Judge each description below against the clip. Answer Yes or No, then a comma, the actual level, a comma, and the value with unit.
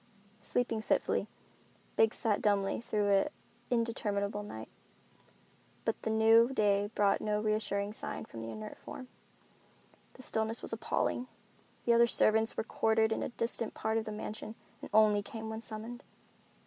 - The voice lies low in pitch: No, high, 220 Hz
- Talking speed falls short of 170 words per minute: Yes, average, 150 wpm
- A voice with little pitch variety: Yes, narrow, 1.6 semitones